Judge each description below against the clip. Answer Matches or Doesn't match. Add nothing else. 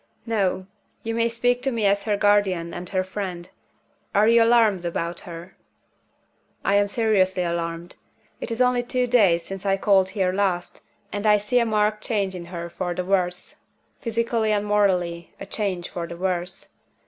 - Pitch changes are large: Doesn't match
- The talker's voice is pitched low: Doesn't match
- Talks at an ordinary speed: Matches